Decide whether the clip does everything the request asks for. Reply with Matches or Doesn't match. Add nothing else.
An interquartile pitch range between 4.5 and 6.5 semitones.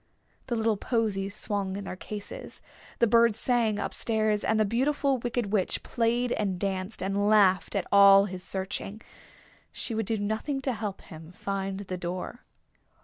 Doesn't match